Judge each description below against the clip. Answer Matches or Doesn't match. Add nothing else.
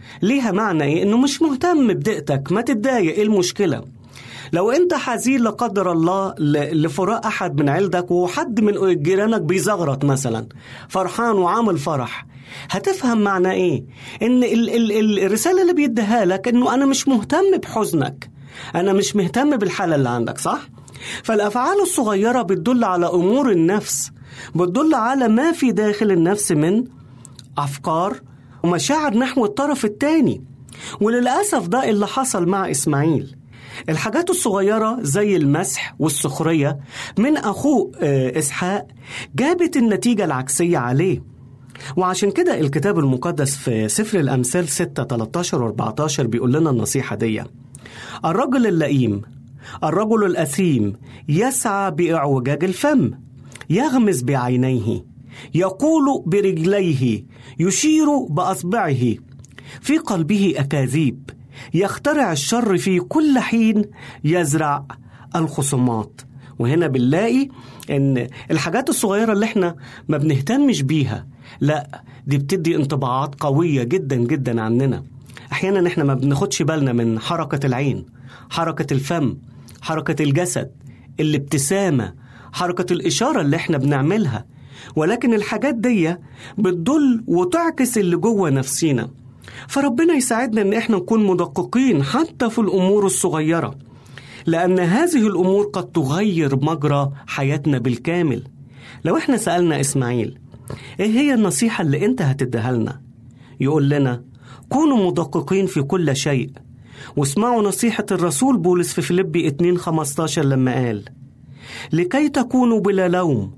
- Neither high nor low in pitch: Matches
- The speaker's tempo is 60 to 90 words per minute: Doesn't match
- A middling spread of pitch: Doesn't match